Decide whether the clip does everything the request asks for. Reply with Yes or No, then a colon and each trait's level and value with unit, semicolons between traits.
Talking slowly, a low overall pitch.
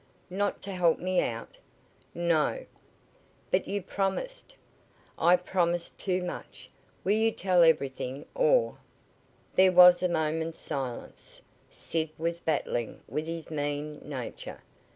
No: slow, 130 wpm; medium, 170 Hz